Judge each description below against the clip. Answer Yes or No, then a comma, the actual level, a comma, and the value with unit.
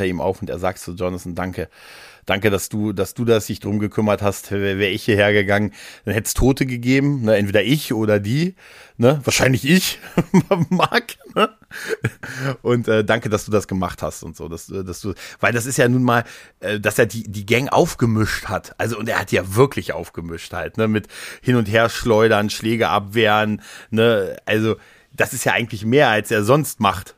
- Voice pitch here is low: Yes, low, 110 Hz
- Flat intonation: No, average, 3.2 semitones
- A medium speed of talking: No, fast, 200 wpm